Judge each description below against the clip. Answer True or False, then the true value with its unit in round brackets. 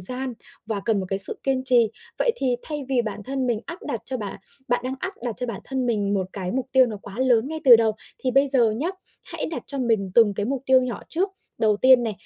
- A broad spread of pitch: False (3.4 semitones)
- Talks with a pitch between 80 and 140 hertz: False (245 Hz)